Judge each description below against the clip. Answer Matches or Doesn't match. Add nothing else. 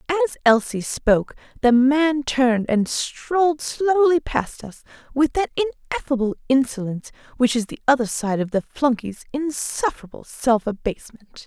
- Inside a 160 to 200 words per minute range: Doesn't match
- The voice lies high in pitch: Matches